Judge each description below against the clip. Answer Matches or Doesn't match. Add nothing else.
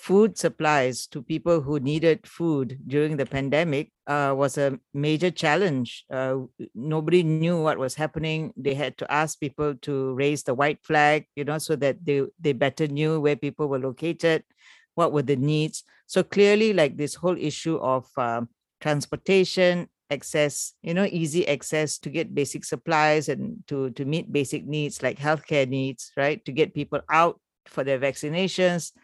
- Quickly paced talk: Doesn't match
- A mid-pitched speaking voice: Matches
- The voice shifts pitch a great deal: Doesn't match